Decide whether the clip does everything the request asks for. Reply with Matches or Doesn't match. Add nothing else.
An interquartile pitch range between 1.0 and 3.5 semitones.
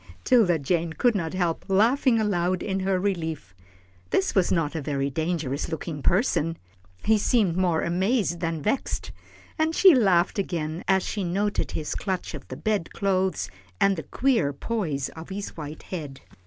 Doesn't match